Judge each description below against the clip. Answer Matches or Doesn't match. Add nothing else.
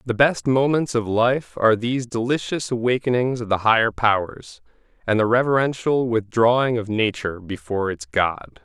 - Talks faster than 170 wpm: Doesn't match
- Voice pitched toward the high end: Doesn't match